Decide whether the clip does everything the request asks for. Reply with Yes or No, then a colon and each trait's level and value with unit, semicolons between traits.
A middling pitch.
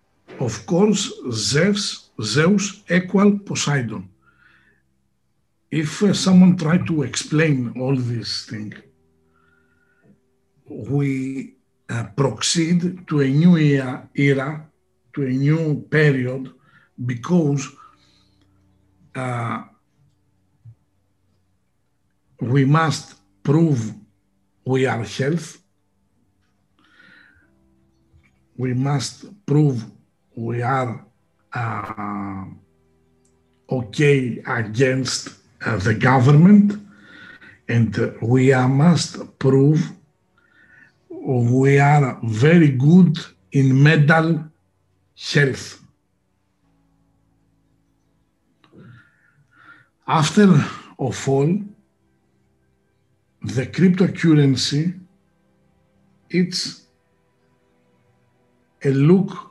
No: low, 130 Hz